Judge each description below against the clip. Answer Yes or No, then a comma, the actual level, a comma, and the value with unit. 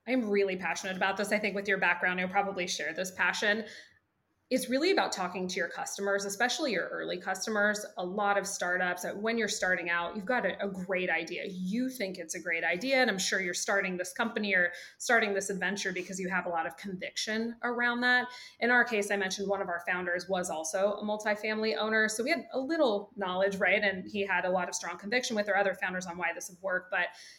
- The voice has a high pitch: Yes, high, 200 Hz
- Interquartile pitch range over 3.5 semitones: No, average, 3.0 semitones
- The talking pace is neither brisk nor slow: No, fast, 230 wpm